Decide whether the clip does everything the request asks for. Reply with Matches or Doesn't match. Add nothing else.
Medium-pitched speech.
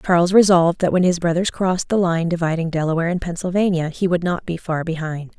Matches